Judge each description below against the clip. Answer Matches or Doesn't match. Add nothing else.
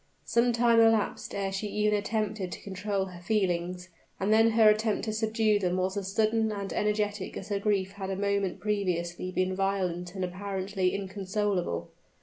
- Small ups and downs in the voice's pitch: Matches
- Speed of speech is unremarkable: Matches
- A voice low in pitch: Doesn't match